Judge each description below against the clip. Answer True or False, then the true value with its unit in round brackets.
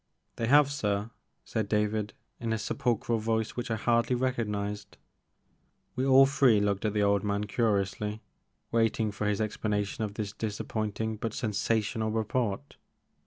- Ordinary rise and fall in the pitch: False (2.0 semitones)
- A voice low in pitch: True (110 Hz)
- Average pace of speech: True (145 wpm)